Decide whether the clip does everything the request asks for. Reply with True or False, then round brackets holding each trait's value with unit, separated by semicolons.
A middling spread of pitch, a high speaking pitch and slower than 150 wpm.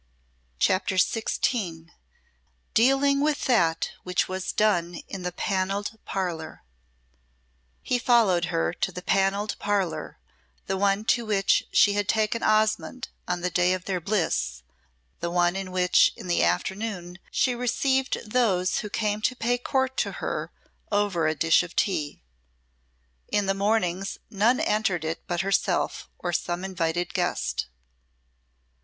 True (3.5 semitones; 195 Hz; 140 wpm)